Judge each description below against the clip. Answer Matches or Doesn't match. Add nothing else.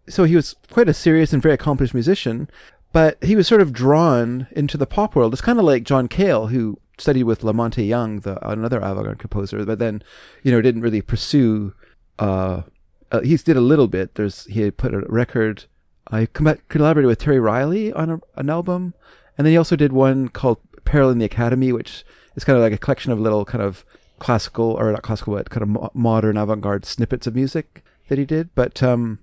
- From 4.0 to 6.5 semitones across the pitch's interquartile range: Matches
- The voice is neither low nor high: Doesn't match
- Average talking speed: Doesn't match